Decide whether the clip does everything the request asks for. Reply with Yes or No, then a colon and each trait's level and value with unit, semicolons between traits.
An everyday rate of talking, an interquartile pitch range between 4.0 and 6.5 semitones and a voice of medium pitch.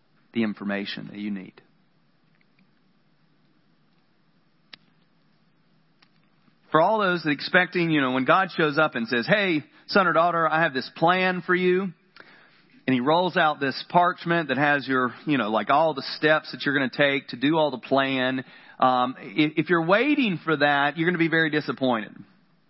Yes: average, 175 wpm; average, 4.9 semitones; medium, 155 Hz